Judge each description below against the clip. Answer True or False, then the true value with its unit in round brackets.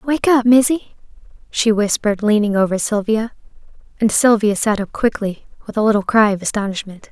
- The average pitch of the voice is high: True (215 Hz)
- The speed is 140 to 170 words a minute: True (160 wpm)